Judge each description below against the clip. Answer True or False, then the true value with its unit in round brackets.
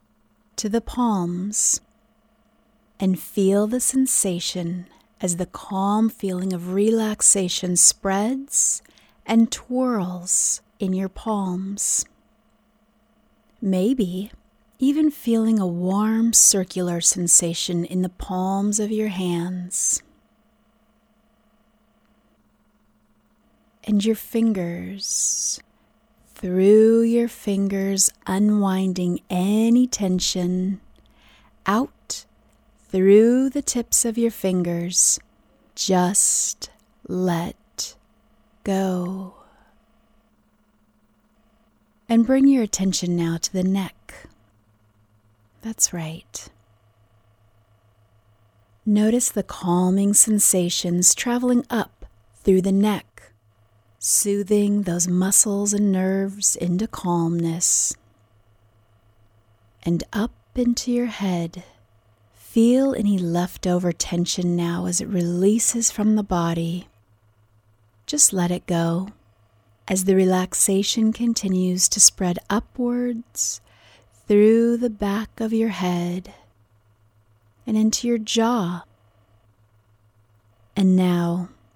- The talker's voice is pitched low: False (190 Hz)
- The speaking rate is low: True (85 wpm)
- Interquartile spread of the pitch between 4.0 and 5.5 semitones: True (4.5 semitones)